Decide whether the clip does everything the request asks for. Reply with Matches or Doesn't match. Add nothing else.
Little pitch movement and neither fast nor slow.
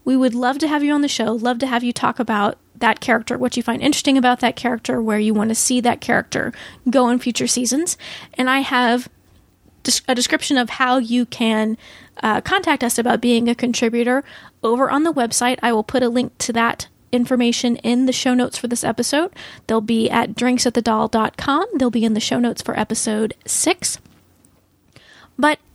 Matches